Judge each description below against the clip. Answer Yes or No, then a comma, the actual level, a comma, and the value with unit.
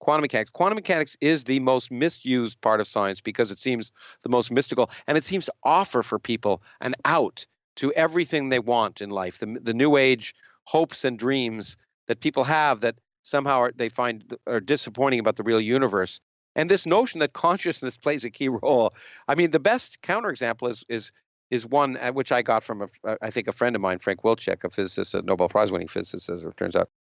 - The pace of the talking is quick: Yes, fast, 210 wpm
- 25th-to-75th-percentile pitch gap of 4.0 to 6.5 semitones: Yes, average, 4.3 semitones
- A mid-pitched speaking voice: No, low, 125 Hz